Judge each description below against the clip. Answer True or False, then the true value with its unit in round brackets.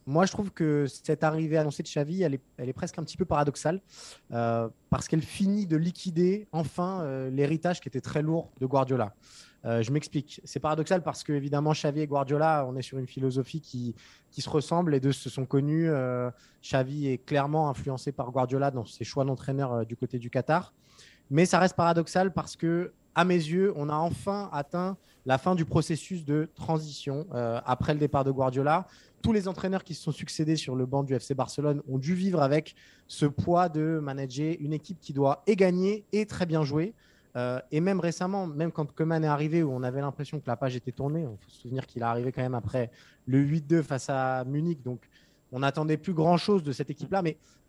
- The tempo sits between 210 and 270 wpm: True (215 wpm)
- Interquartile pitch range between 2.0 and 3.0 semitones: False (3.7 semitones)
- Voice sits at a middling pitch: True (150 Hz)